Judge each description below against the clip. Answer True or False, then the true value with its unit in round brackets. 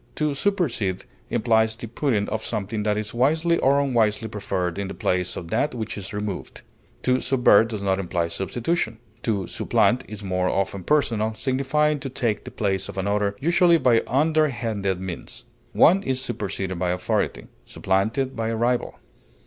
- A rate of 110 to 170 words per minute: True (165 wpm)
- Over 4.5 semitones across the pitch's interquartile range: True (5.3 semitones)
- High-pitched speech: False (110 Hz)